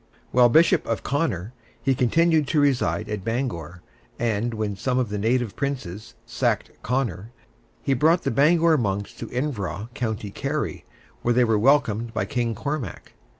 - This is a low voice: Yes, low, 120 Hz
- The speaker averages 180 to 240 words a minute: No, average, 155 wpm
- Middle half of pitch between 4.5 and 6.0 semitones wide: Yes, average, 4.9 semitones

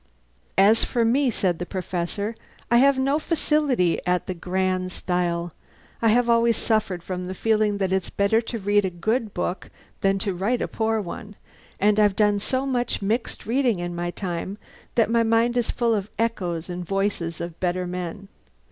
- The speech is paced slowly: No, average, 185 wpm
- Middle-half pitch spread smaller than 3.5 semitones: No, average, 4.1 semitones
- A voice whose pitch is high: Yes, high, 205 Hz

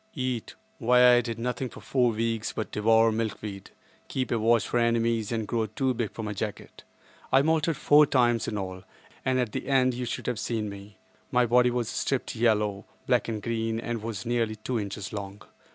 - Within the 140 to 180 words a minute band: No, fast, 205 wpm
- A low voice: Yes, low, 115 Hz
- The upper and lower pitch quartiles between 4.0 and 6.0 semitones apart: No, narrow, 2.5 semitones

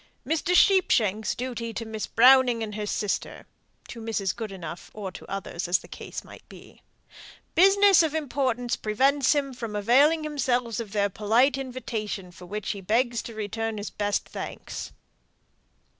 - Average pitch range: Yes, average, 4.2 semitones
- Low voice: No, high, 230 Hz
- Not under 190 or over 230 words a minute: No, average, 155 wpm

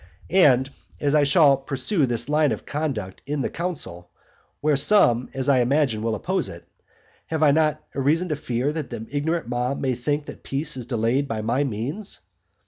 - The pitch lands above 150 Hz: No, medium, 140 Hz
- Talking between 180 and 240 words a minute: Yes, average, 185 wpm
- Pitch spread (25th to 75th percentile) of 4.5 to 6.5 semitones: No, average, 3.7 semitones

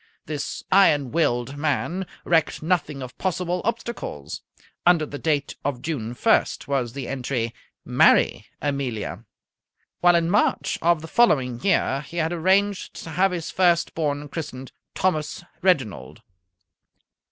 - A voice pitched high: No, medium, 155 Hz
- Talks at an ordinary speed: No, slow, 130 wpm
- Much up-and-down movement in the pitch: No, average, 4.6 semitones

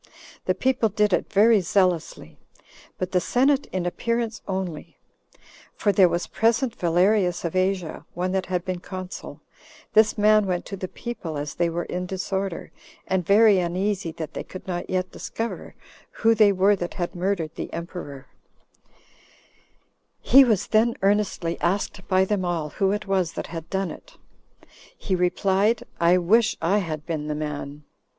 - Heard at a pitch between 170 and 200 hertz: Yes, medium, 185 Hz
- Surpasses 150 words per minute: Yes, average, 160 wpm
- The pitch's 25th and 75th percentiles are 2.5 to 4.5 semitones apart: Yes, average, 3.1 semitones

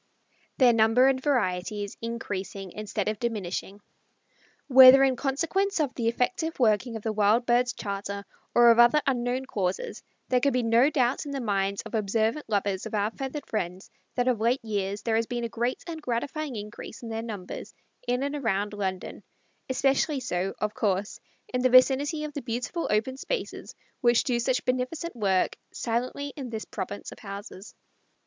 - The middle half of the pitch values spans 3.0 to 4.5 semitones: Yes, average, 4.0 semitones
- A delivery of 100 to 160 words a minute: No, average, 175 wpm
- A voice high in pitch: Yes, high, 235 Hz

